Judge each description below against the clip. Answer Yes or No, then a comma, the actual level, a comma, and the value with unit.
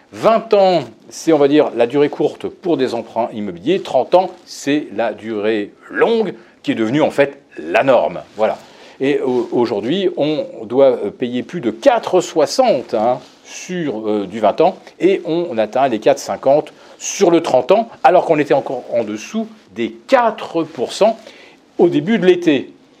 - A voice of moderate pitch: Yes, medium, 160 Hz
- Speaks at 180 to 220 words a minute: No, average, 165 wpm